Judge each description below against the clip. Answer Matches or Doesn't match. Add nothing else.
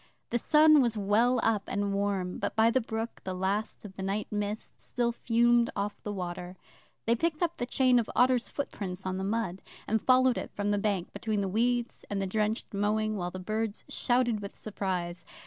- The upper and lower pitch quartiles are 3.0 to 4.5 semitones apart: Matches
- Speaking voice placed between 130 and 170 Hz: Doesn't match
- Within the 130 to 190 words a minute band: Doesn't match